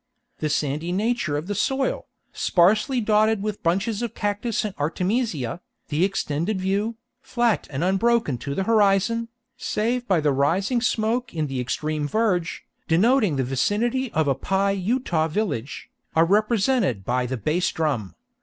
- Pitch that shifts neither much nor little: No, wide, 6.5 semitones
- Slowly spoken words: No, average, 150 wpm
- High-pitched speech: Yes, high, 195 Hz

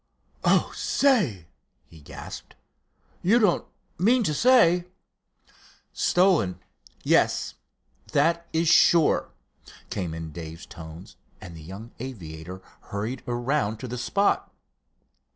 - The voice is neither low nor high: No, low, 120 Hz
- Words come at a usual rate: No, slow, 105 wpm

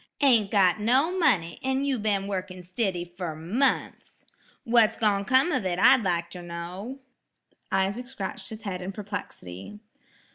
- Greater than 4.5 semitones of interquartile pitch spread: Yes, average, 5.1 semitones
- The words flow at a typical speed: Yes, average, 150 wpm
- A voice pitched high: Yes, high, 200 Hz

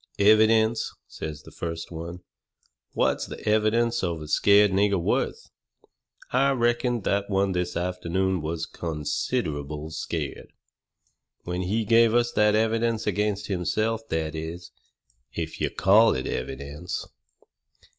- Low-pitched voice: Yes, very low, 95 Hz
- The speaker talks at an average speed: No, slow, 125 wpm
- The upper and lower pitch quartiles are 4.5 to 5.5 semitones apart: Yes, average, 4.9 semitones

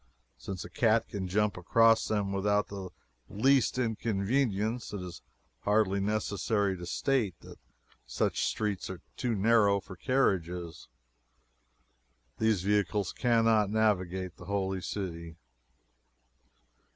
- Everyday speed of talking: No, slow, 115 wpm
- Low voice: Yes, low, 100 Hz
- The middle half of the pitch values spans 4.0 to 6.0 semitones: No, average, 2.8 semitones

